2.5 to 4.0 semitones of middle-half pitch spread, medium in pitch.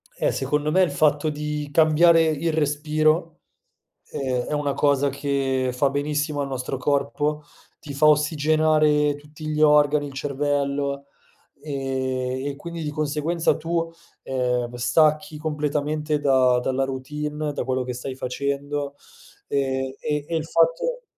No: narrow, 2.0 semitones; medium, 145 Hz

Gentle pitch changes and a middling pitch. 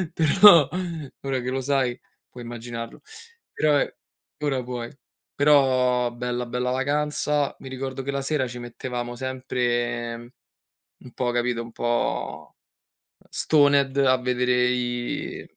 No: narrow, 2.1 semitones; low, 125 Hz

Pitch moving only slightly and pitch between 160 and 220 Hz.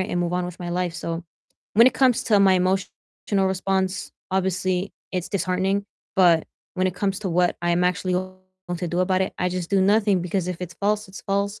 Yes: narrow, 1.5 semitones; medium, 185 Hz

